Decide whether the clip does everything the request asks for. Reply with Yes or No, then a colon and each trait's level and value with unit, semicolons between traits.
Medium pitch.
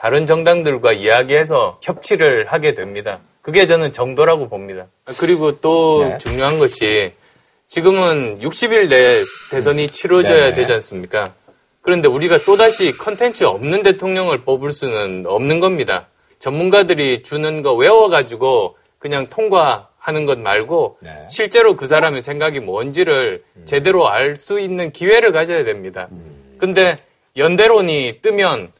No: high, 195 Hz